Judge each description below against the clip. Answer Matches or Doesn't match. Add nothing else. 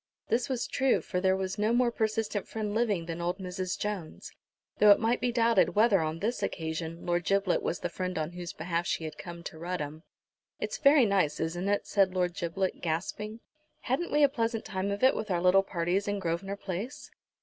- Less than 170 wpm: Doesn't match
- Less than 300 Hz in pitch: Matches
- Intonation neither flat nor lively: Matches